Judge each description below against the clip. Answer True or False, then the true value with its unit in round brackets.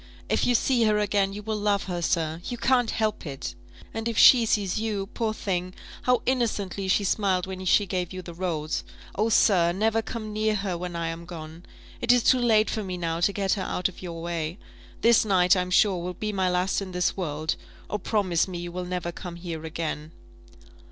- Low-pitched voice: False (185 Hz)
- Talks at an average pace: False (215 wpm)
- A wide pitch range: False (3.7 semitones)